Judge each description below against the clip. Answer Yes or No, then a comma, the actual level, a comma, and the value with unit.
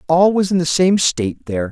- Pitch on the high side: No, medium, 165 Hz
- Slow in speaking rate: No, fast, 245 wpm